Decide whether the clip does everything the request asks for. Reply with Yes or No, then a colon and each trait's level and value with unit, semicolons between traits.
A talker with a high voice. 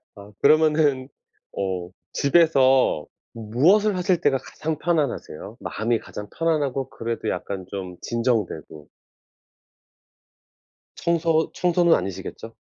No: low, 135 Hz